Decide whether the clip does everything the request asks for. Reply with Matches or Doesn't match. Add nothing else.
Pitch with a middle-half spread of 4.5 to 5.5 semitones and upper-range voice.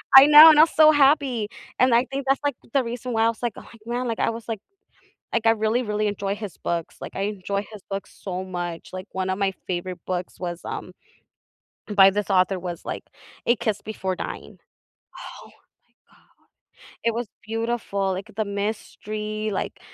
Doesn't match